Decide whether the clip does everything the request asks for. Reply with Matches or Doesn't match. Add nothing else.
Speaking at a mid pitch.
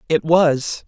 Matches